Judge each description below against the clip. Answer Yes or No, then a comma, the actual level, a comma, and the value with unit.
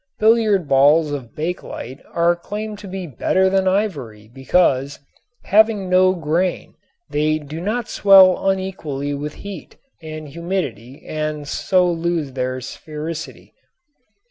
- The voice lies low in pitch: No, medium, 165 Hz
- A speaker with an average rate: No, slow, 120 wpm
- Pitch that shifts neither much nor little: Yes, average, 4.7 semitones